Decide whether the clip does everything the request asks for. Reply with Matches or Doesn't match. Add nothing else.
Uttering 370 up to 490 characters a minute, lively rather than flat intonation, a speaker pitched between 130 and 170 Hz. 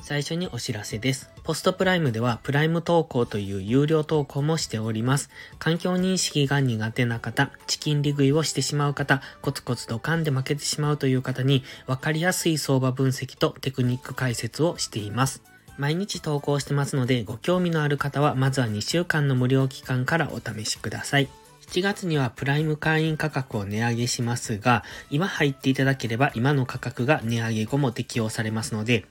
Doesn't match